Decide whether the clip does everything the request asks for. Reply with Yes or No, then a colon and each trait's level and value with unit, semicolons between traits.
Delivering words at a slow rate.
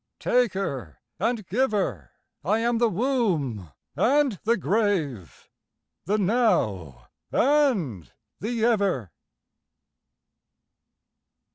Yes: slow, 80 wpm